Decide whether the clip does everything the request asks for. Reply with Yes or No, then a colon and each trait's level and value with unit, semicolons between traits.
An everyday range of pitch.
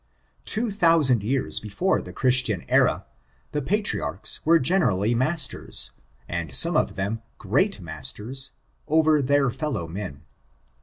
No: wide, 7.7 semitones